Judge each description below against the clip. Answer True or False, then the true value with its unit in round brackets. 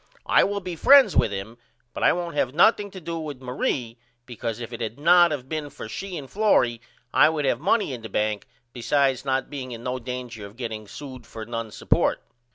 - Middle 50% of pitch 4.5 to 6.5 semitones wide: True (5.3 semitones)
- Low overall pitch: True (130 Hz)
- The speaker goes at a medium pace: False (215 wpm)